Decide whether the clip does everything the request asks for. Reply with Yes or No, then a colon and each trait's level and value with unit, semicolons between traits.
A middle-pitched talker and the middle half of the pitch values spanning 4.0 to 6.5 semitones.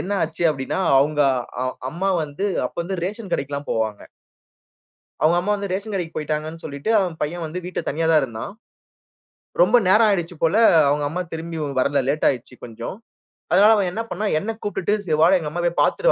Yes: medium, 165 Hz; average, 4.5 semitones